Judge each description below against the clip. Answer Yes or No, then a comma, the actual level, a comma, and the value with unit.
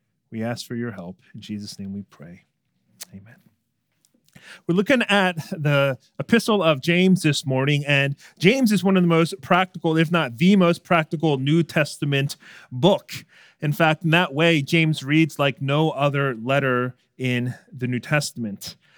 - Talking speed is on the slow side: No, average, 160 wpm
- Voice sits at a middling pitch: Yes, medium, 150 Hz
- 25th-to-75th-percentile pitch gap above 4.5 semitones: Yes, average, 5.1 semitones